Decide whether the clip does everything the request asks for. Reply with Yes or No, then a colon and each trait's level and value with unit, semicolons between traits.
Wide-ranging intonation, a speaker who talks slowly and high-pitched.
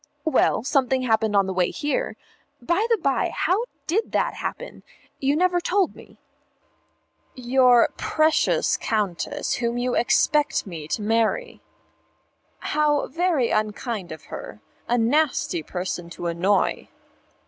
Yes: wide, 6.9 semitones; slow, 125 wpm; high, 245 Hz